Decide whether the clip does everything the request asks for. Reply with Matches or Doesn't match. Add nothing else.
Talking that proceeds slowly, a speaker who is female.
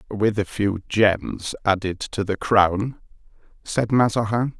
Doesn't match